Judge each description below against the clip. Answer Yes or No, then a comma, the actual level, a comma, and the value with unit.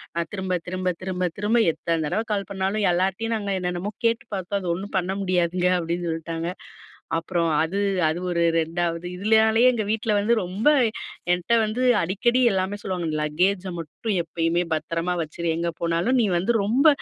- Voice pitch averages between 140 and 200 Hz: Yes, medium, 185 Hz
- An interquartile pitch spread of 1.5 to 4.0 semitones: Yes, average, 3.4 semitones